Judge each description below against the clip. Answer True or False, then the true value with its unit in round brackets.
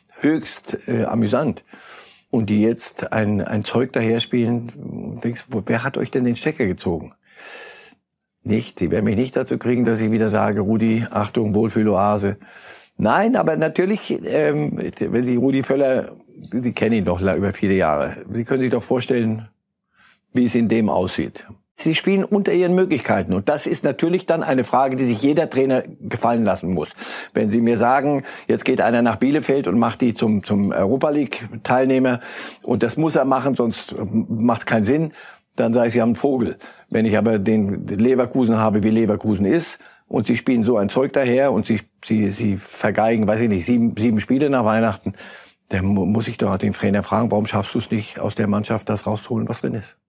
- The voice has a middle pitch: False (115 Hz)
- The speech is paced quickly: True (195 wpm)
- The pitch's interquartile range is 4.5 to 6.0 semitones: False (3.4 semitones)